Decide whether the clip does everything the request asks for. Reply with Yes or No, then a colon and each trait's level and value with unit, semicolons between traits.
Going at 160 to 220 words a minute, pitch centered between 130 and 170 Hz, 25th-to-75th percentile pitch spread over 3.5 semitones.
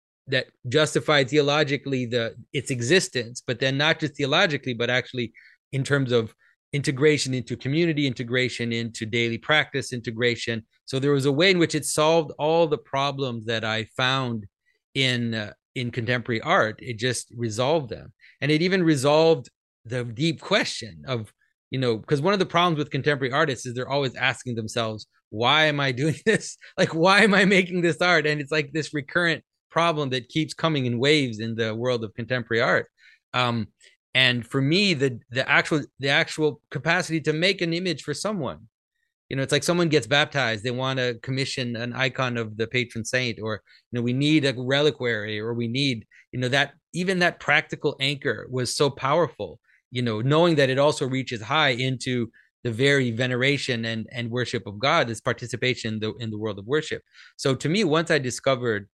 Yes: average, 190 wpm; low, 135 Hz; average, 4.1 semitones